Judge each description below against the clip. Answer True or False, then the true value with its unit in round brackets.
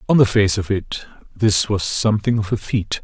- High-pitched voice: False (105 Hz)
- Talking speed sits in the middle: False (215 wpm)